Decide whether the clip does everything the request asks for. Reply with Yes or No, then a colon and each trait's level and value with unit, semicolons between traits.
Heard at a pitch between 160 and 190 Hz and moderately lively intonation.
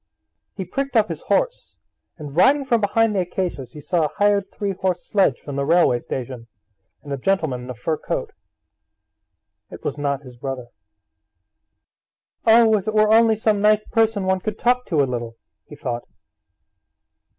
No: medium, 185 Hz; wide, 7.6 semitones